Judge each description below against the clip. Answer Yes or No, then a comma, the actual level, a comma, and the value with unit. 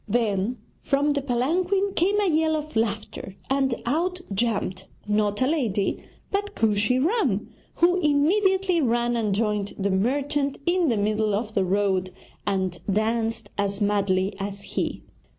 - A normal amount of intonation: No, wide, 7.1 semitones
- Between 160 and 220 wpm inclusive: No, average, 145 wpm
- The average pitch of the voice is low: No, high, 235 Hz